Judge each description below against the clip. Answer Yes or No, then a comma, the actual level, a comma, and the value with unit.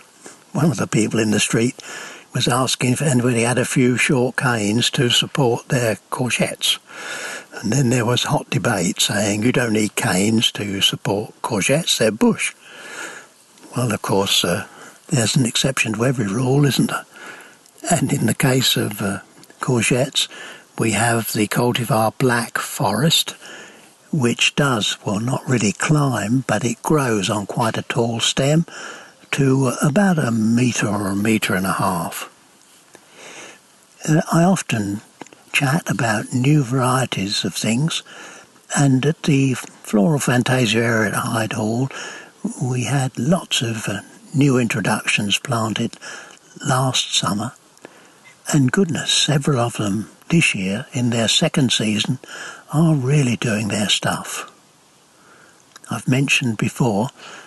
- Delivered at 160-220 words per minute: No, slow, 135 wpm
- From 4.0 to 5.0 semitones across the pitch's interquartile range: Yes, average, 4.4 semitones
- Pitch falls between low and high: No, low, 125 Hz